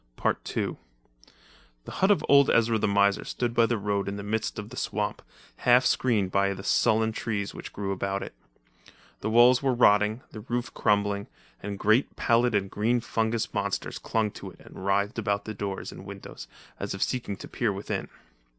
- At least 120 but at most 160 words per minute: No, average, 185 wpm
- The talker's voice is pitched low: Yes, low, 105 Hz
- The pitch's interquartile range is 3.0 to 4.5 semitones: No, narrow, 2.6 semitones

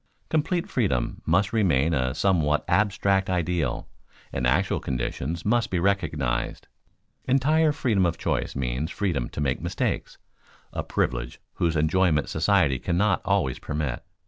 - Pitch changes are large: Yes, wide, 6.5 semitones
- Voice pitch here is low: Yes, very low, 85 Hz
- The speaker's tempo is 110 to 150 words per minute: Yes, slow, 135 wpm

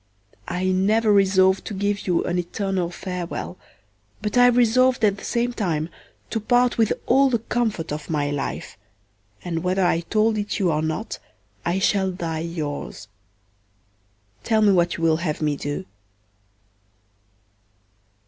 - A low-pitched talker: No, high, 190 Hz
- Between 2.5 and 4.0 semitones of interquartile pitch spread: No, average, 4.4 semitones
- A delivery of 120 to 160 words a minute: Yes, average, 150 wpm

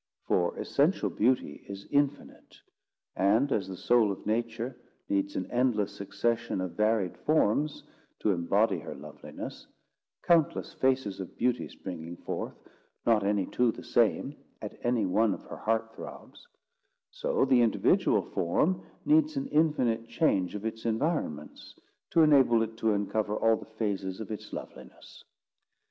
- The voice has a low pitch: Yes, low, 115 Hz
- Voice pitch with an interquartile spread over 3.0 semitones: Yes, average, 4.7 semitones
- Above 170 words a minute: No, average, 145 wpm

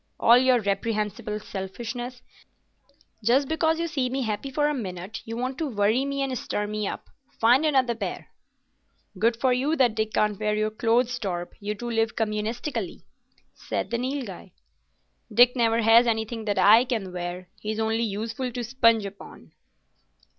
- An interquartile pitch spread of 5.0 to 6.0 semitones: No, average, 3.0 semitones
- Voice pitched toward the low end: No, high, 230 Hz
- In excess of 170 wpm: No, average, 165 wpm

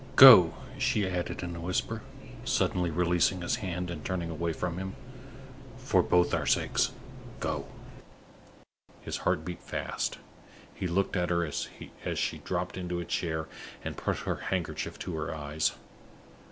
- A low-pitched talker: Yes, very low, 90 Hz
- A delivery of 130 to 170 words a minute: Yes, average, 150 wpm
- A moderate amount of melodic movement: No, narrow, 1.6 semitones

